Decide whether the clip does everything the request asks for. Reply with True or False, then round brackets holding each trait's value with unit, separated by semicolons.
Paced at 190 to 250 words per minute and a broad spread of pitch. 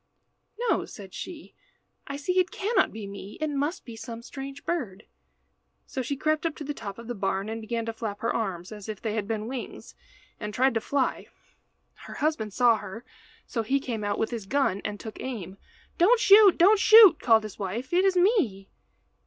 True (200 wpm; 6.1 semitones)